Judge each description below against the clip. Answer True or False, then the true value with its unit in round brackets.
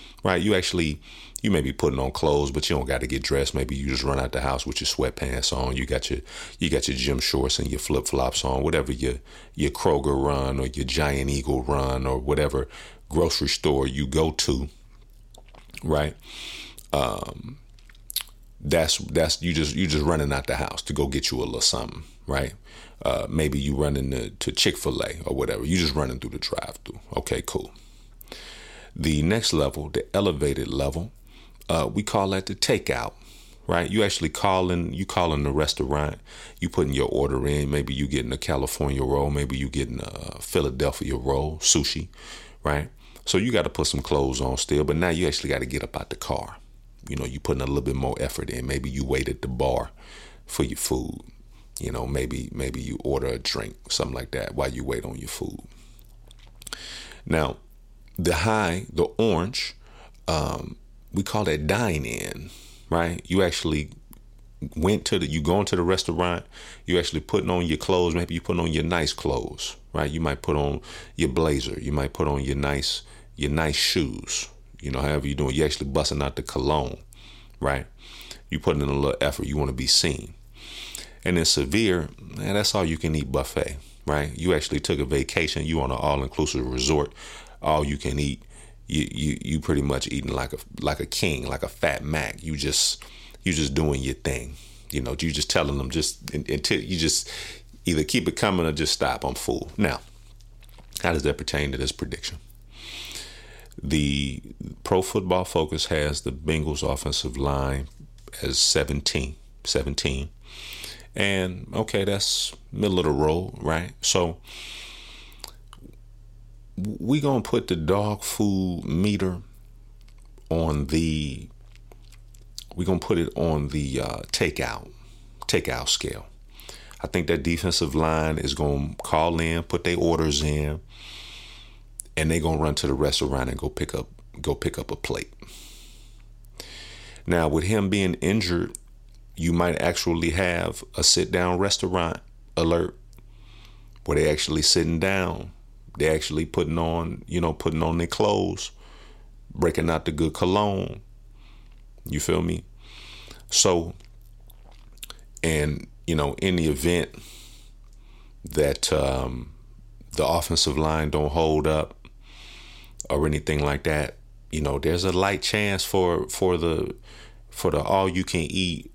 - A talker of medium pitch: False (85 Hz)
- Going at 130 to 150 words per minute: False (170 wpm)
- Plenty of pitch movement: True (6.7 semitones)